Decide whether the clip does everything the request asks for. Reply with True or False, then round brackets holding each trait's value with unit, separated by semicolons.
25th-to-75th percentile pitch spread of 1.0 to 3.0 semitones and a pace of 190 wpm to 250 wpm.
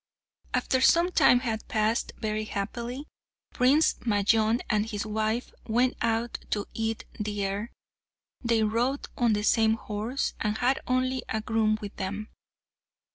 False (2.4 semitones; 140 wpm)